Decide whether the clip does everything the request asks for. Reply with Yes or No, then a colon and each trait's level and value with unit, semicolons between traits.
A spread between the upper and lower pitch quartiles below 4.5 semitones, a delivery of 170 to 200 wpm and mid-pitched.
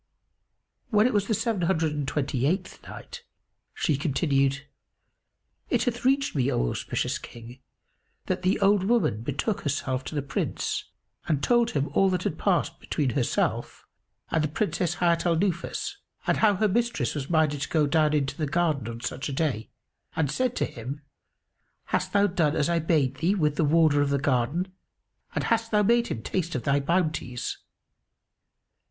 No: wide, 5.6 semitones; average, 175 wpm; medium, 160 Hz